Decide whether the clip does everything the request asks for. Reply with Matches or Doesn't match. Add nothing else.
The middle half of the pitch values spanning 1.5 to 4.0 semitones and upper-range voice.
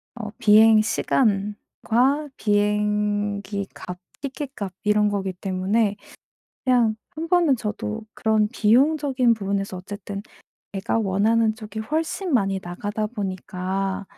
Matches